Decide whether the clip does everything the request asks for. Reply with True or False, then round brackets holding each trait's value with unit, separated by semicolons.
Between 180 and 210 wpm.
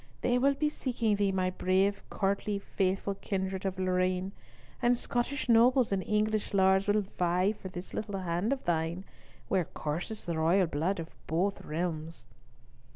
False (155 wpm)